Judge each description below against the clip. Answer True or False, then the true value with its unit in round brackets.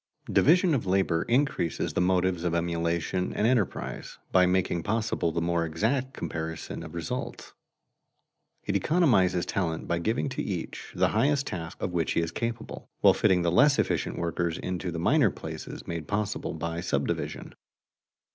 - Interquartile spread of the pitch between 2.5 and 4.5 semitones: False (5.1 semitones)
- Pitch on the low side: True (90 Hz)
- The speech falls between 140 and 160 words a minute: True (155 wpm)